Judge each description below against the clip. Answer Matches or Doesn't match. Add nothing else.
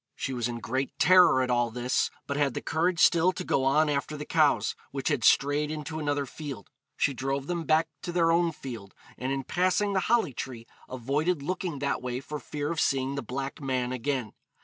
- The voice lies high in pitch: Doesn't match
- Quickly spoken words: Matches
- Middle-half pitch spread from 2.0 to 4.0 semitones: Matches